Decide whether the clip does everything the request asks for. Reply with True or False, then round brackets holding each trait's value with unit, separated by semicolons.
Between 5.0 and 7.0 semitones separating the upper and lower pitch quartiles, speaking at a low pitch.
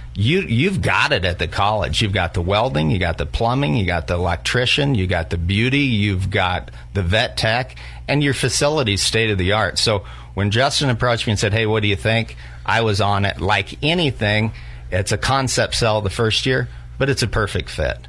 True (5.3 semitones; 105 Hz)